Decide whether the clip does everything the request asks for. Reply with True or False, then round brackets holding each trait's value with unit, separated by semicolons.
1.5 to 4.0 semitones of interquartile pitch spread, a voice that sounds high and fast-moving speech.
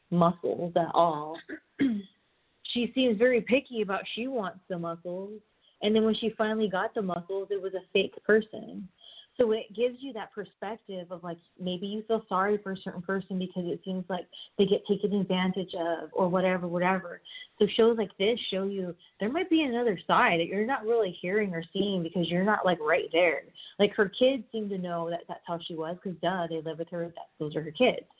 True (3.6 semitones; 195 Hz; 210 wpm)